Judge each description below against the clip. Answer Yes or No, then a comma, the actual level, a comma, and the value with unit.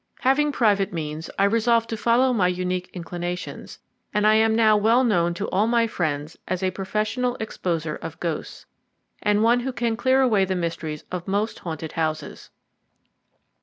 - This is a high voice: Yes, high, 200 Hz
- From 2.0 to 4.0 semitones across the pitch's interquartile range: No, average, 4.8 semitones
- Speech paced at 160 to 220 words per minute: Yes, average, 165 wpm